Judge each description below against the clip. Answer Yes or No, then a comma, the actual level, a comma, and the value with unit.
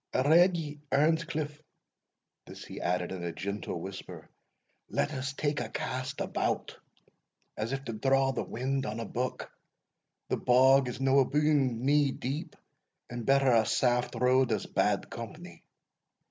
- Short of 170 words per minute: Yes, average, 150 wpm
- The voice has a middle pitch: No, low, 130 Hz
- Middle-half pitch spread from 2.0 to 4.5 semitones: Yes, average, 3.0 semitones